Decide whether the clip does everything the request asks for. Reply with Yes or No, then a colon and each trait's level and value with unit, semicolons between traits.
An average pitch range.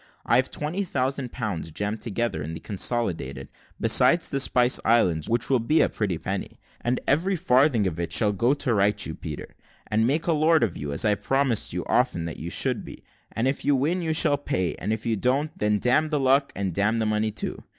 No: wide, 5.7 semitones